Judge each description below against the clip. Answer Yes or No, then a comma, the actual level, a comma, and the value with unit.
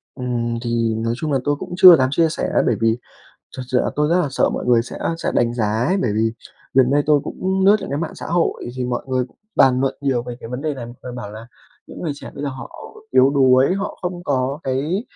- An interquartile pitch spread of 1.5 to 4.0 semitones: Yes, average, 3.7 semitones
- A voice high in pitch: No, low, 130 Hz